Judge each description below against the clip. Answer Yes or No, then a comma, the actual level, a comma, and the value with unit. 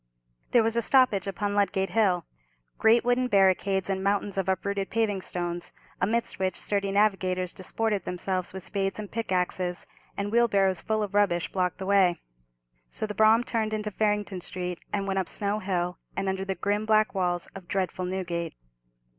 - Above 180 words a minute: No, average, 170 wpm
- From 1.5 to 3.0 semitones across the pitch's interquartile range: Yes, narrow, 2.4 semitones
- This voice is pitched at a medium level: No, high, 195 Hz